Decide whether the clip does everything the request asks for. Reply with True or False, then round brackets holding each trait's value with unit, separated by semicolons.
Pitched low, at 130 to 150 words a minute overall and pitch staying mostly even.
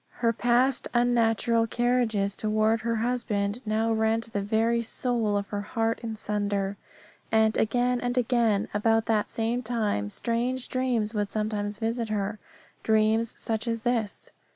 False (225 Hz; 145 wpm; 2.0 semitones)